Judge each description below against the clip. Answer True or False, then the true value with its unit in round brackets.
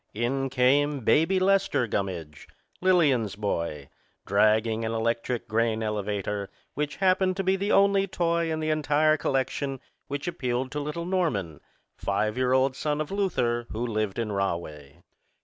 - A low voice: True (130 Hz)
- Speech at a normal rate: True (150 wpm)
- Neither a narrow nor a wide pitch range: False (6.6 semitones)